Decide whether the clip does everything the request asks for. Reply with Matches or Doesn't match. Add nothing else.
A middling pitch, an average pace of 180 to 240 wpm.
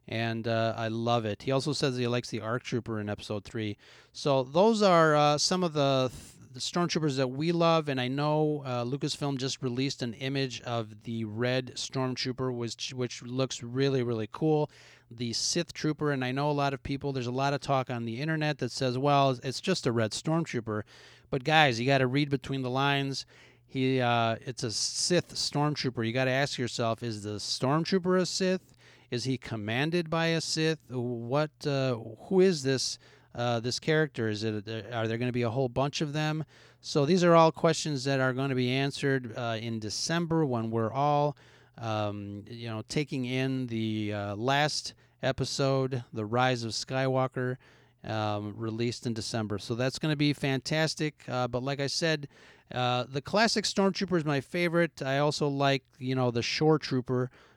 Doesn't match